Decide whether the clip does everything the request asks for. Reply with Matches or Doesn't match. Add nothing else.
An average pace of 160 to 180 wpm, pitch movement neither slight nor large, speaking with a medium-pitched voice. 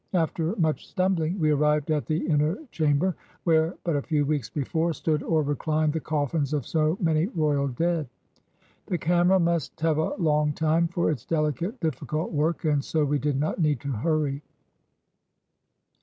Doesn't match